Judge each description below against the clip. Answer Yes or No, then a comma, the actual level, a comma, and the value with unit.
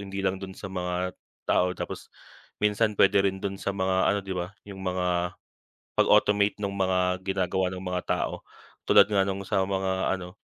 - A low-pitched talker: Yes, very low, 95 Hz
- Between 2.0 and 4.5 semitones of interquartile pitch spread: No, narrow, 1.3 semitones